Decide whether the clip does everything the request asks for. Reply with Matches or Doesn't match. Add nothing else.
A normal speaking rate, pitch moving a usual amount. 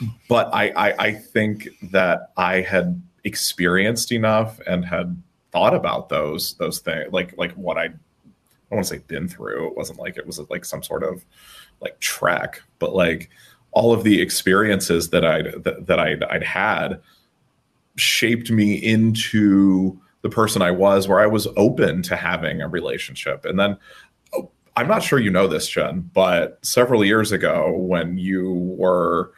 Matches